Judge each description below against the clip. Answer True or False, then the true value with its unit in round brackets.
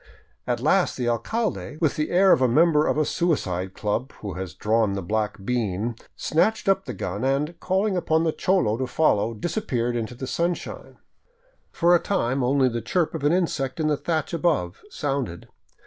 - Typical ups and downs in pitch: False (6.8 semitones)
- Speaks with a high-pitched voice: False (135 Hz)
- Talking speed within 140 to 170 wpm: False (185 wpm)